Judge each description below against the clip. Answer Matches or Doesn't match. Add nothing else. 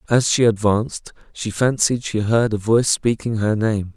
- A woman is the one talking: Doesn't match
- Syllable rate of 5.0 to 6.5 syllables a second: Doesn't match